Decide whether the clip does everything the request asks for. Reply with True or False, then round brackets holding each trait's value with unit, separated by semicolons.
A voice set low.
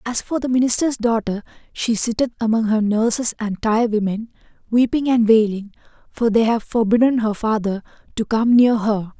False (225 Hz)